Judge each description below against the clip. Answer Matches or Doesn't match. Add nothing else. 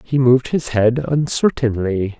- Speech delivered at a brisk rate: Doesn't match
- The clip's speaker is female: Doesn't match